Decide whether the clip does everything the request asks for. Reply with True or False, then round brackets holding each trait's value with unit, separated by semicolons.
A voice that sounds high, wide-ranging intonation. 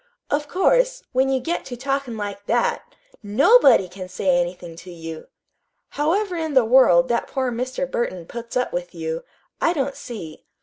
True (245 Hz; 7.1 semitones)